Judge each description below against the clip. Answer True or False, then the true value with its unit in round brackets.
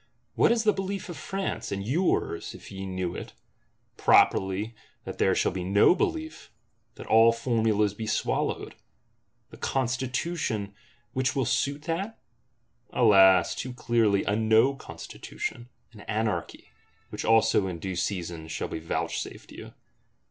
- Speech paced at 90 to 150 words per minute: True (135 wpm)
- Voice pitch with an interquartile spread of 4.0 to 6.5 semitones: True (5.5 semitones)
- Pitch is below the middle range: True (110 Hz)